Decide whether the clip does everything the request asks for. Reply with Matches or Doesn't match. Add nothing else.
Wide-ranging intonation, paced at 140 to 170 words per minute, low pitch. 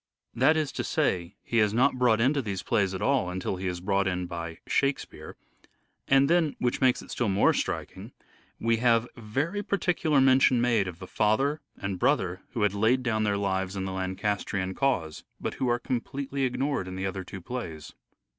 Doesn't match